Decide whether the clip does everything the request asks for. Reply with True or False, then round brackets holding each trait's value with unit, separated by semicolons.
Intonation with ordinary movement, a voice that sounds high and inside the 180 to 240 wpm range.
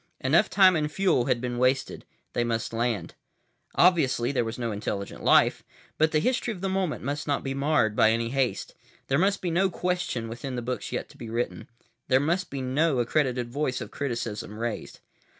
False (5.0 semitones; 130 Hz; 195 wpm)